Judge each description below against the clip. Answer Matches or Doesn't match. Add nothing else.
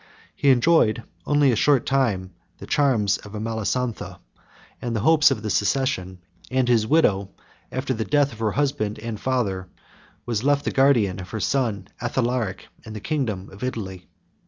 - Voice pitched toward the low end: Matches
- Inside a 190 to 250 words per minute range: Doesn't match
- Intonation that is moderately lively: Matches